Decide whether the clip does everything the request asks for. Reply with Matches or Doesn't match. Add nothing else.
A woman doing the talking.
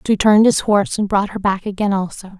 Matches